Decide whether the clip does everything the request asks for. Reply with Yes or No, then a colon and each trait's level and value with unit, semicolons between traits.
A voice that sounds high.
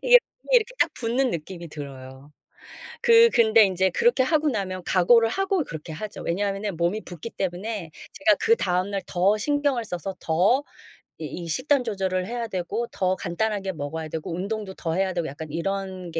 Yes: high, 195 Hz